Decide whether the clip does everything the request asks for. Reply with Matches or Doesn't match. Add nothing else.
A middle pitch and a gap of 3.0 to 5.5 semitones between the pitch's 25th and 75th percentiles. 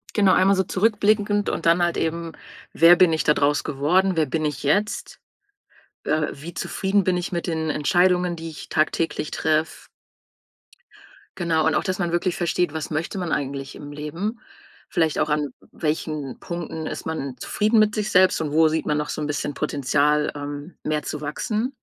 Matches